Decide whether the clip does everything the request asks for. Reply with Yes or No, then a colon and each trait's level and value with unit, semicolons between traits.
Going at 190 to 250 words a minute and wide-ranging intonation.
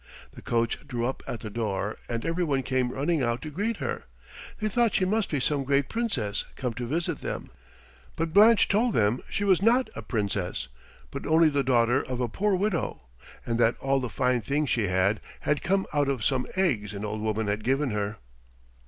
Yes: fast, 205 wpm; wide, 6.6 semitones